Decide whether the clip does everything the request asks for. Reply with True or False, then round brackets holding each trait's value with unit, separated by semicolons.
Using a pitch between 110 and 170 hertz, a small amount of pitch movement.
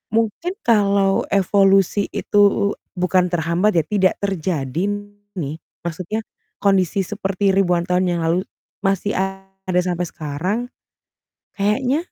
False (195 Hz; 2.3 semitones)